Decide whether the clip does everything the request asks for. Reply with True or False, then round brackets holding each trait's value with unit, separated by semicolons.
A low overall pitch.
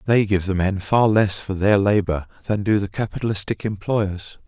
True (100 Hz)